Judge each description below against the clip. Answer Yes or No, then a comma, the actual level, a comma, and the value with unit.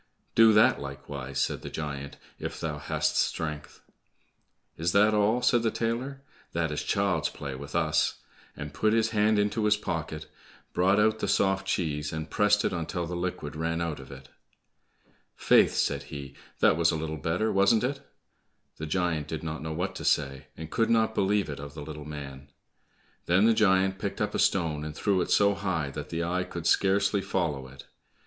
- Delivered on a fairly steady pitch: No, wide, 5.4 semitones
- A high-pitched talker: No, very low, 85 Hz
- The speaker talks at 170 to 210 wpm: Yes, average, 190 wpm